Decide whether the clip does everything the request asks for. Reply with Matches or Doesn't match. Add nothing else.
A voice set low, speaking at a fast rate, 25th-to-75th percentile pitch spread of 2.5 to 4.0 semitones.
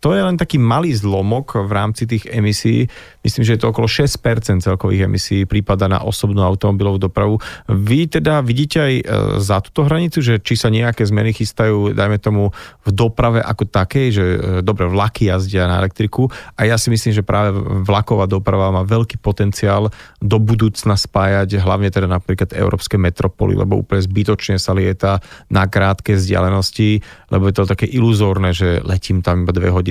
Matches